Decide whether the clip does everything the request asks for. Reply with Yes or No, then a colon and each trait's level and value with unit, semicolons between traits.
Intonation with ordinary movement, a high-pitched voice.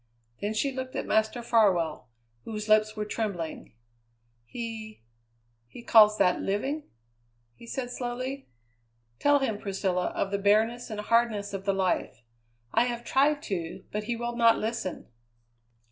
Yes: average, 3.0 semitones; high, 220 Hz